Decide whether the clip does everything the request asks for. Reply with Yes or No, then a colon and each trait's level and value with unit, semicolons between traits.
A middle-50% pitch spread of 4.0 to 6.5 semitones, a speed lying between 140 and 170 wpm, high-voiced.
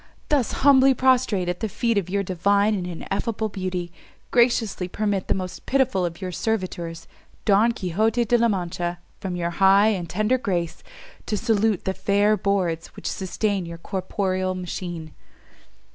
No: average, 3.5 semitones; average, 155 wpm; high, 195 Hz